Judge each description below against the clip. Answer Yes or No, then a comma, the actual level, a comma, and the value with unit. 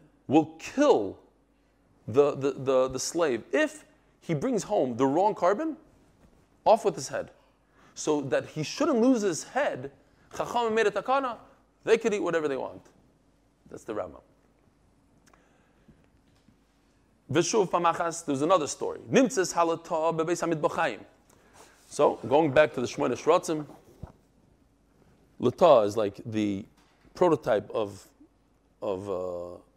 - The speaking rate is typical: No, slow, 105 wpm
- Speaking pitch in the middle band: Yes, medium, 165 Hz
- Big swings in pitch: Yes, wide, 7.1 semitones